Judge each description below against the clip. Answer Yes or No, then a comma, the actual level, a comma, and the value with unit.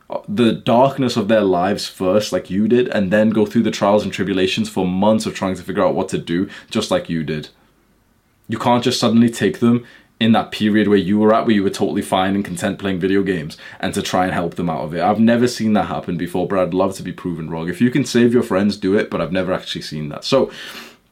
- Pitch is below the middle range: Yes, low, 105 Hz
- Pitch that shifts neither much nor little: Yes, average, 3.6 semitones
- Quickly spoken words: Yes, fast, 260 wpm